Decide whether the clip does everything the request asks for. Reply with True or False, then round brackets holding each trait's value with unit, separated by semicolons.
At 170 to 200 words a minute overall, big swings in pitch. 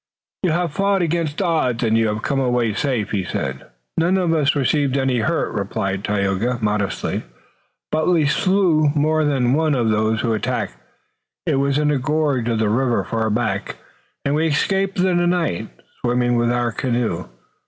True (175 wpm; 5.8 semitones)